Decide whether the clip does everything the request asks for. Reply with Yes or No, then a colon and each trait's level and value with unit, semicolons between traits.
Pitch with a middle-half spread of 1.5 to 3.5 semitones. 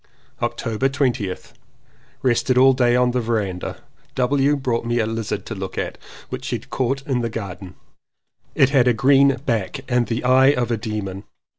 Yes: average, 3.1 semitones